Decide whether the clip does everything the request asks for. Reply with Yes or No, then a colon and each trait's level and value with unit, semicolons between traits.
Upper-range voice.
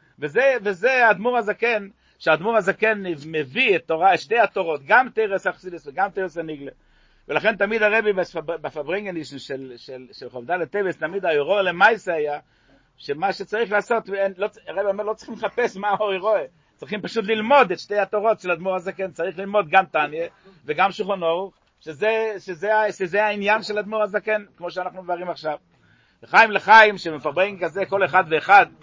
Yes: high, 195 Hz